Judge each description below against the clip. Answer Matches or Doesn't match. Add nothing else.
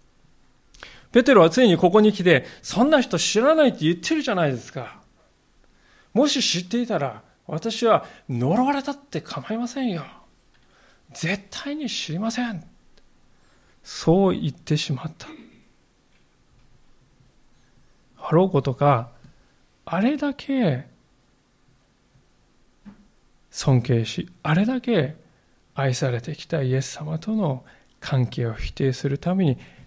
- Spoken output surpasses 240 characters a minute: Doesn't match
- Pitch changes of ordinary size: Doesn't match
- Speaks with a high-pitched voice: Doesn't match